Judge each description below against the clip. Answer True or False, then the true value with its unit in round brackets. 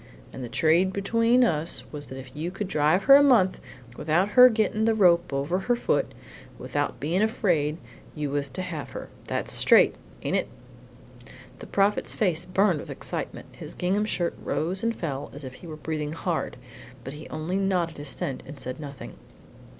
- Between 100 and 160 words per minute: False (185 wpm)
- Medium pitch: True (170 Hz)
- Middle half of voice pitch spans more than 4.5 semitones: True (5.0 semitones)